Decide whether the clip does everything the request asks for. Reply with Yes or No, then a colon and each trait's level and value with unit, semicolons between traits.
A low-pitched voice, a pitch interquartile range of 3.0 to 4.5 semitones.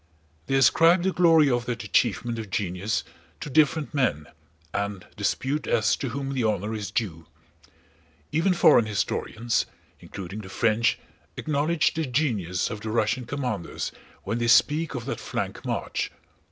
No: low, 120 Hz; wide, 5.4 semitones